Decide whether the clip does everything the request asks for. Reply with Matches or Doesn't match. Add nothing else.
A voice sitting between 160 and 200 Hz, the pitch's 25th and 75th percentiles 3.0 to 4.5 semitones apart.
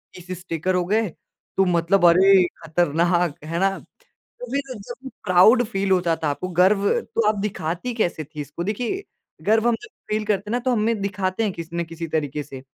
Matches